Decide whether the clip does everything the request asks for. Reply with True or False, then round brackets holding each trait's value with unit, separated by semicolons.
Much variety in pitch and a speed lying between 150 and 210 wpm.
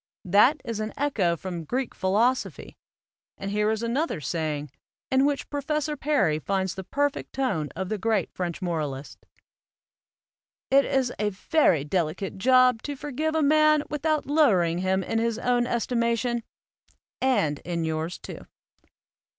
False (7.2 semitones; 140 wpm)